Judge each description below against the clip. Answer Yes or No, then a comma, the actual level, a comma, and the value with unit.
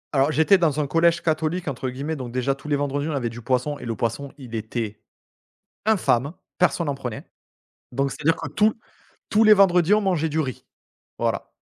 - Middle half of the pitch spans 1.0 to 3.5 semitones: No, average, 4.7 semitones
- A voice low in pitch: No, medium, 145 Hz